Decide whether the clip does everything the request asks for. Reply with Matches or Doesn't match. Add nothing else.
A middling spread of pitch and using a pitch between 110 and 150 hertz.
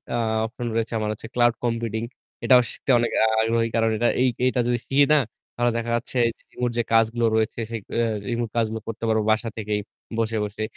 Doesn't match